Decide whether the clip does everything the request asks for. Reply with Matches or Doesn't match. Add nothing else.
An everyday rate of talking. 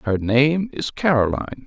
Matches